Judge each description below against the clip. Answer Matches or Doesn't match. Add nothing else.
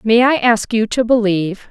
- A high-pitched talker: Matches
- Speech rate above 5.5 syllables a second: Doesn't match